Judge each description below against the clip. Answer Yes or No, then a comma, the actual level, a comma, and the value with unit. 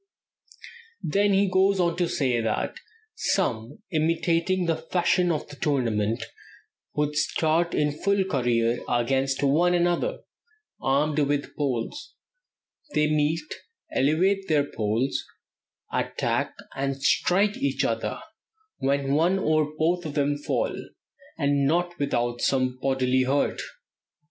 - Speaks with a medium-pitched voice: Yes, medium, 150 Hz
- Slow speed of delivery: Yes, slow, 120 wpm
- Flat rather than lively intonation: No, average, 4.5 semitones